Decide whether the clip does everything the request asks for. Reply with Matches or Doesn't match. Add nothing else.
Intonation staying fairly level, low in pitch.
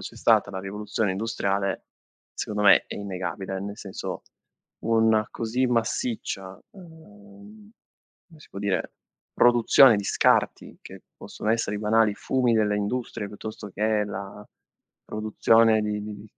Matches